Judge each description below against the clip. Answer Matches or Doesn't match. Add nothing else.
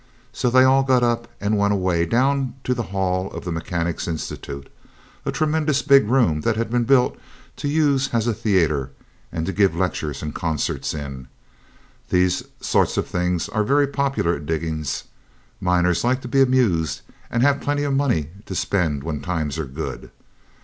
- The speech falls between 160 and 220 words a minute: Matches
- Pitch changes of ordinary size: Doesn't match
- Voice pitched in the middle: Doesn't match